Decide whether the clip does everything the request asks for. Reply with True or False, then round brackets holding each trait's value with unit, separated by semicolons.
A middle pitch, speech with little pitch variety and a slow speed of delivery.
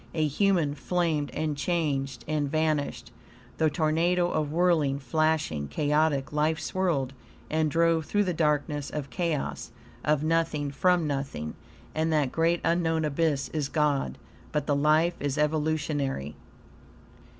True (155 Hz; 2.2 semitones; 130 wpm)